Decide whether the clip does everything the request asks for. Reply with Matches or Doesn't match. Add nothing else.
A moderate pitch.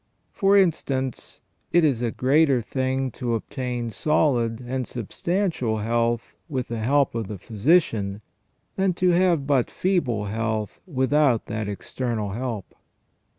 Doesn't match